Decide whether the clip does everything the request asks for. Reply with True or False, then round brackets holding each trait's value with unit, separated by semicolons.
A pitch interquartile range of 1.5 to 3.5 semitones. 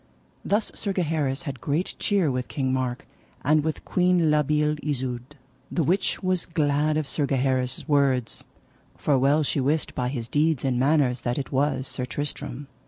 True (3.0 semitones)